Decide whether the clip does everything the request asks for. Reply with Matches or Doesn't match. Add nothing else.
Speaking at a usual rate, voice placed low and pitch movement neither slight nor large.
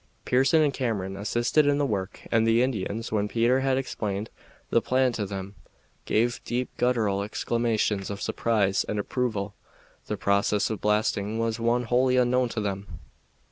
Matches